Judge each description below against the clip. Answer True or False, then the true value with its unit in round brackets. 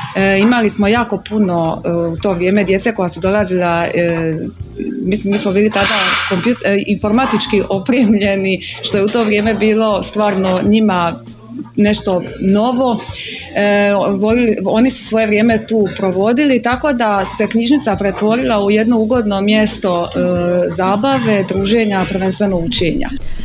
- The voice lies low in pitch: False (205 Hz)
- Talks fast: False (120 wpm)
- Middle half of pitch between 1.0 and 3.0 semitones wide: True (2.5 semitones)